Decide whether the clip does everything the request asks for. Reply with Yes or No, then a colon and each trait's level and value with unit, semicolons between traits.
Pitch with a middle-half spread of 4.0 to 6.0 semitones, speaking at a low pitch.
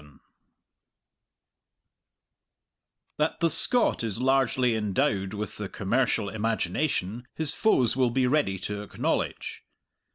Yes: average, 4.6 semitones; low, 120 Hz